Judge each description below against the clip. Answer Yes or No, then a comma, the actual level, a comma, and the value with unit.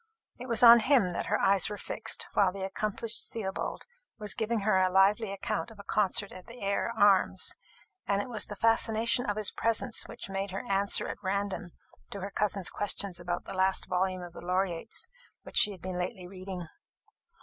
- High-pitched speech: Yes, high, 200 Hz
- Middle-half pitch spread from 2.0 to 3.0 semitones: Yes, narrow, 2.4 semitones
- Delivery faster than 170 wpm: Yes, average, 195 wpm